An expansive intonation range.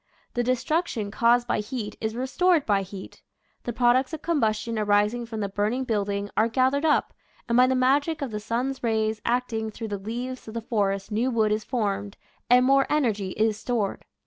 No: average, 3.3 semitones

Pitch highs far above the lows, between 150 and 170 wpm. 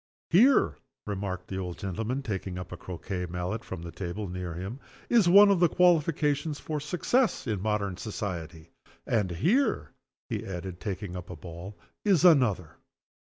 Yes: wide, 8.7 semitones; average, 160 wpm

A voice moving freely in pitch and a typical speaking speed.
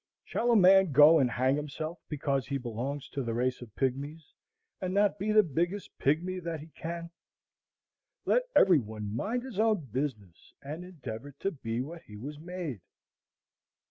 Yes: wide, 5.7 semitones; average, 170 wpm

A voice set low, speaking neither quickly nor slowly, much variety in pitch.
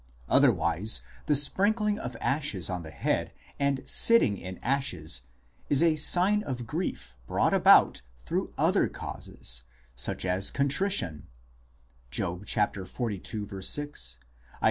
No: low, 120 Hz; slow, 110 wpm; wide, 8.4 semitones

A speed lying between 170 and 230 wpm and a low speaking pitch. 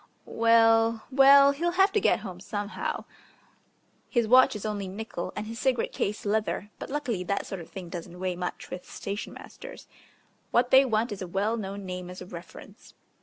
No: average, 185 wpm; high, 210 Hz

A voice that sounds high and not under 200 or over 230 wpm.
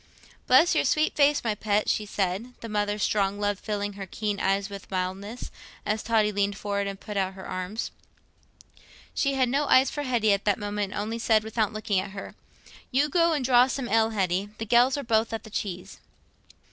Yes: high, 210 Hz; fast, 205 wpm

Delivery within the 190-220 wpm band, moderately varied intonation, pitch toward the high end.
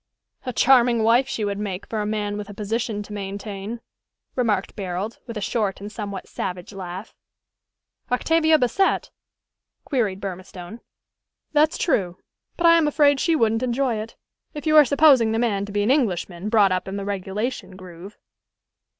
No: average, 165 wpm; average, 4.1 semitones; high, 215 Hz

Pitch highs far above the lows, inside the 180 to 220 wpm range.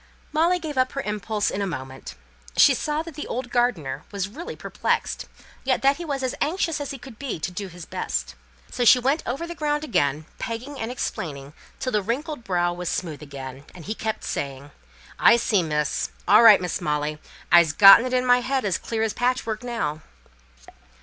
Yes: wide, 7.8 semitones; average, 200 wpm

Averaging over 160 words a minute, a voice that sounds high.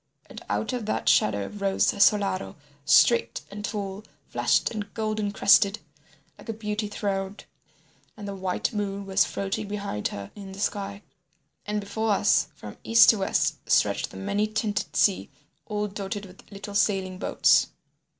No: average, 155 wpm; high, 205 Hz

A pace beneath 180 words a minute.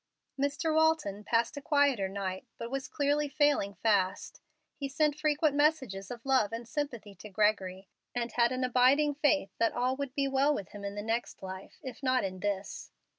No: average, 185 wpm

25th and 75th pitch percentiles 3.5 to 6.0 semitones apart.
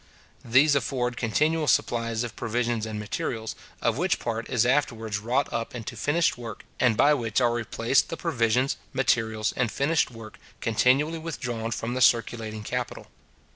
No: average, 2.9 semitones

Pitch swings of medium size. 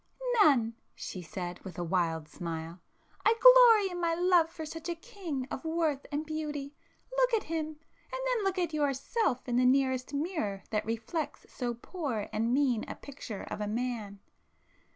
No: wide, 7.3 semitones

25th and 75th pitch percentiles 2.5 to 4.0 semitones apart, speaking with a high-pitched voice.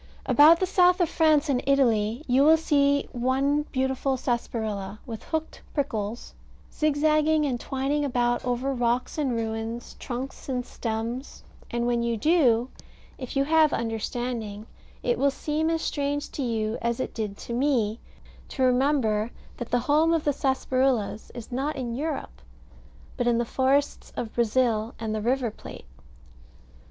Yes: average, 3.6 semitones; very high, 255 Hz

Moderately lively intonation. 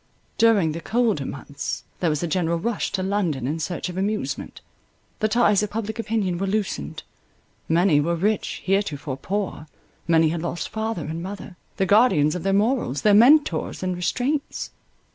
Yes: average, 4.8 semitones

